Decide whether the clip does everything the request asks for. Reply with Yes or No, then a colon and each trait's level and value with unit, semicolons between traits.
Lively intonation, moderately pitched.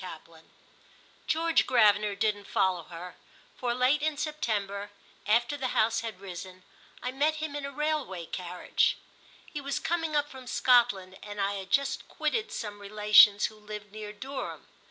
No: wide, 5.8 semitones; high, 215 Hz